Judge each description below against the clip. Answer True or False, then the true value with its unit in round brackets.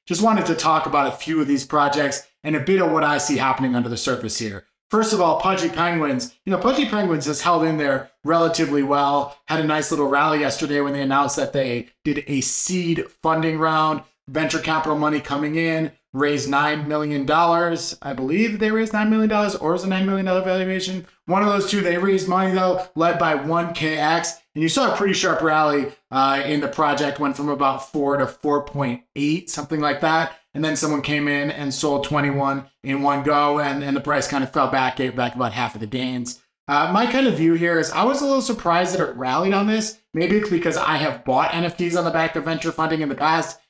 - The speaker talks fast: True (225 wpm)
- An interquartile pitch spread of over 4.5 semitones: False (3.4 semitones)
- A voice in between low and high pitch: True (155 Hz)